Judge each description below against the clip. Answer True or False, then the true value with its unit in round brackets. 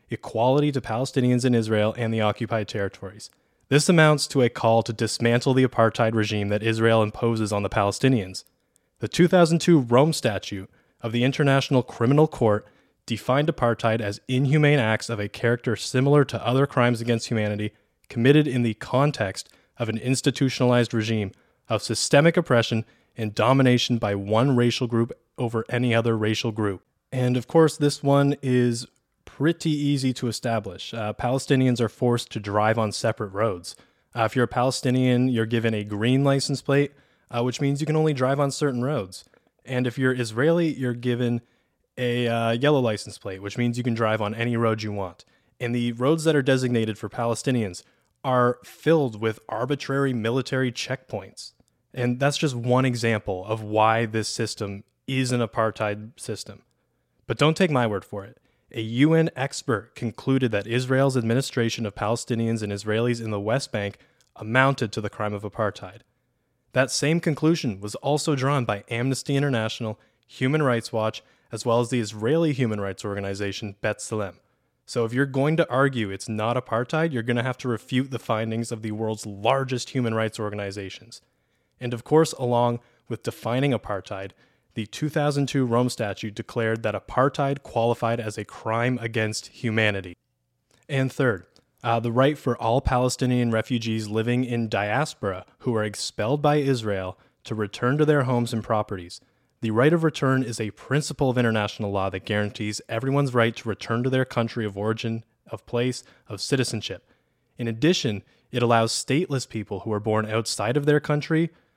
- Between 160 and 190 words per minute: True (170 wpm)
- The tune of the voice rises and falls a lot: False (3.1 semitones)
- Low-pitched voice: True (120 Hz)